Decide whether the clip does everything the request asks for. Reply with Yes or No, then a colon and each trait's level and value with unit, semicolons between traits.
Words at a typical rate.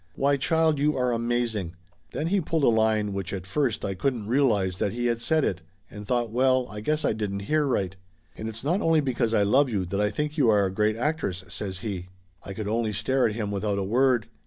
No: fast, 240 wpm